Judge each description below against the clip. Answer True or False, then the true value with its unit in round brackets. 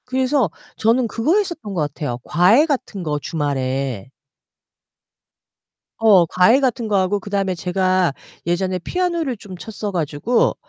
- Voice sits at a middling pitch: False (195 Hz)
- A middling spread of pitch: False (6.1 semitones)